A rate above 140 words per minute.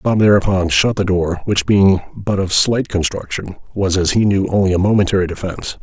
Yes: average, 195 wpm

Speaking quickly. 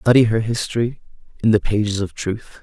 No: average, 185 wpm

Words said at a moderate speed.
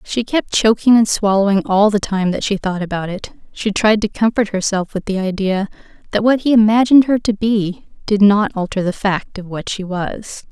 No: fast, 210 wpm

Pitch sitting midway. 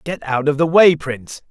Yes: medium, 150 Hz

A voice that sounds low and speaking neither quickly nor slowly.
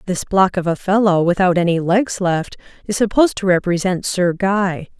No: medium, 185 Hz; average, 180 wpm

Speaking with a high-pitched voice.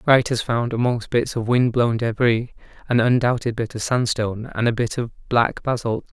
No: low, 120 Hz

